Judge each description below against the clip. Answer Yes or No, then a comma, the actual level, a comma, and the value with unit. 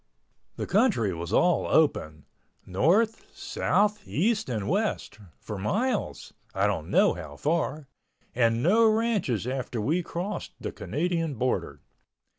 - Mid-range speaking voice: Yes, medium, 160 Hz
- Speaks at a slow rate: Yes, slow, 115 wpm